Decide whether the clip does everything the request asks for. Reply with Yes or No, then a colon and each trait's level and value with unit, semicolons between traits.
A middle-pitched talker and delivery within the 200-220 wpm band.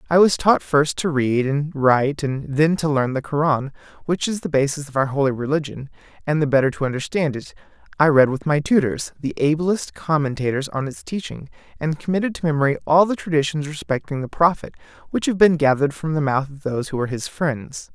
Yes: medium, 150 Hz; fast, 205 wpm